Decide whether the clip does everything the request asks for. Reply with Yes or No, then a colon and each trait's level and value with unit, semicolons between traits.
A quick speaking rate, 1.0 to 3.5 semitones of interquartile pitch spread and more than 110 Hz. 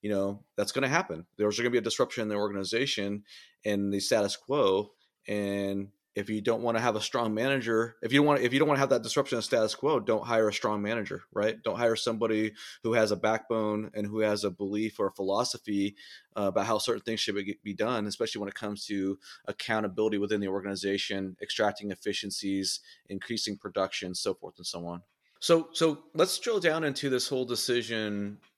No: fast, 210 wpm; narrow, 2.4 semitones; low, 105 Hz